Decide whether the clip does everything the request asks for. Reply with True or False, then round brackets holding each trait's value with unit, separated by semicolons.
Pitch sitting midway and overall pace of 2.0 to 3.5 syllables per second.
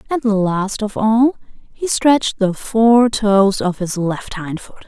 False (210 Hz; 3.4 syllables/s)